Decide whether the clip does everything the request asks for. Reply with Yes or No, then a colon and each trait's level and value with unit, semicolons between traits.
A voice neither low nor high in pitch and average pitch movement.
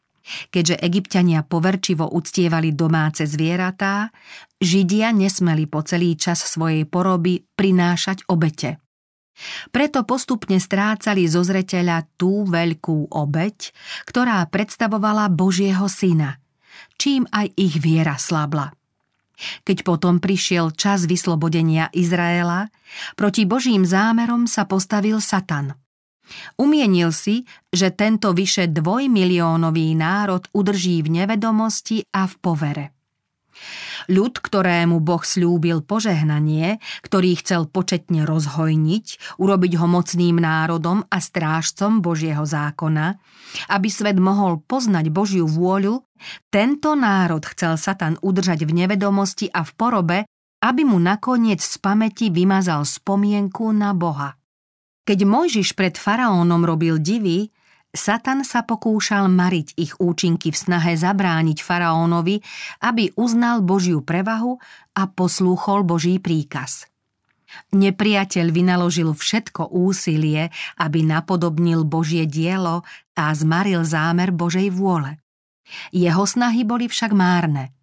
Yes: medium, 180 Hz; average, 3.6 semitones